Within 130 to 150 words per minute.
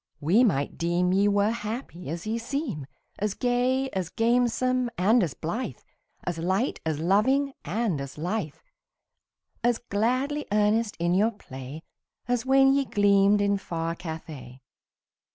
Yes: average, 140 wpm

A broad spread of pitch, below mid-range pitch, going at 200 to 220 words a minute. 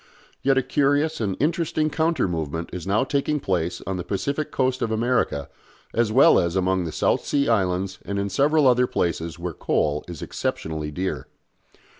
No: wide, 7.8 semitones; low, 100 Hz; average, 175 wpm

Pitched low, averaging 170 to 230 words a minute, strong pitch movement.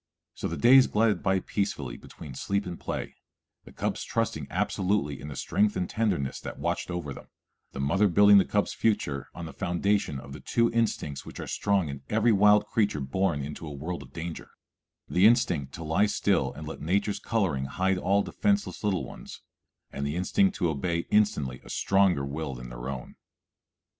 Yes: very low, 90 Hz; average, 190 wpm; wide, 6.2 semitones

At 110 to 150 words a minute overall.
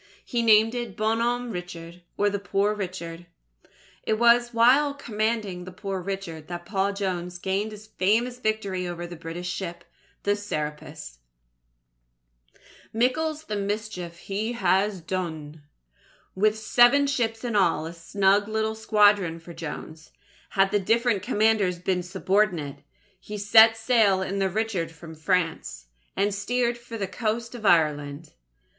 Yes: average, 140 wpm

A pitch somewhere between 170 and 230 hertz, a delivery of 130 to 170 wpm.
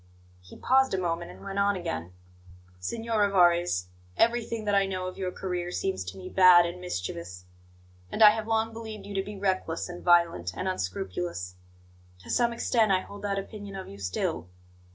No: medium, 185 Hz; average, 185 wpm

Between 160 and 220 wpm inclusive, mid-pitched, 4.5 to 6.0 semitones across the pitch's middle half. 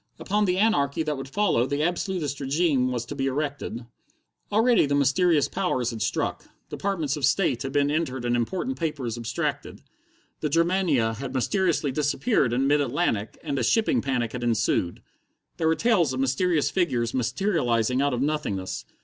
Yes: average, 165 wpm; medium, 145 Hz; average, 5.3 semitones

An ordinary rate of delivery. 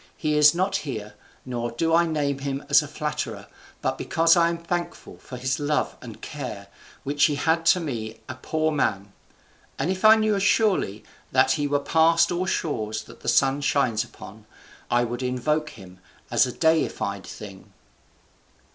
Yes: average, 175 wpm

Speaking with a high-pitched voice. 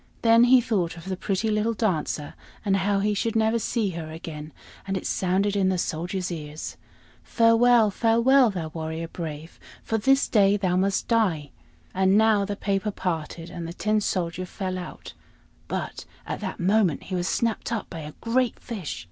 Yes: high, 195 Hz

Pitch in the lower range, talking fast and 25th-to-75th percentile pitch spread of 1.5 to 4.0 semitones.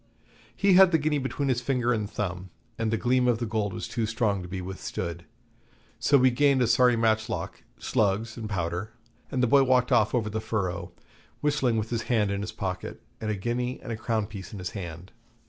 Yes: low, 110 Hz; fast, 215 wpm; average, 3.7 semitones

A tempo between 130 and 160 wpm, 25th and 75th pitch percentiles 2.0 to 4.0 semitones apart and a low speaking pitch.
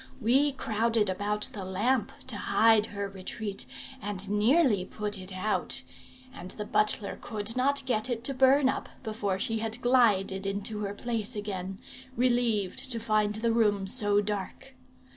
No: average, 155 wpm; average, 2.9 semitones; high, 215 Hz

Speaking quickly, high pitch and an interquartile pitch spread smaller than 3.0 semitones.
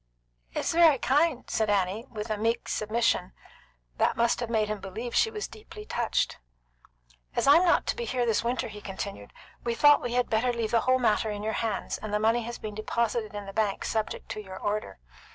Yes: fast, 215 wpm; high, 225 Hz; narrow, 2.6 semitones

